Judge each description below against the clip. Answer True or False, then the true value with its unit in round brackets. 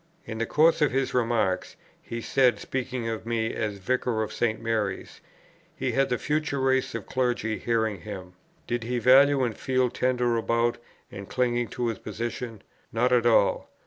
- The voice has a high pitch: False (120 Hz)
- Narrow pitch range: True (2.3 semitones)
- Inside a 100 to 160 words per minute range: False (175 wpm)